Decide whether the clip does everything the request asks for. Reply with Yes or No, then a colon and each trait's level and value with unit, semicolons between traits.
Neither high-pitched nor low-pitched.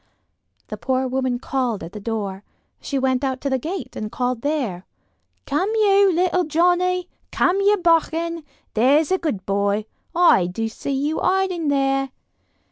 No: very high, 275 Hz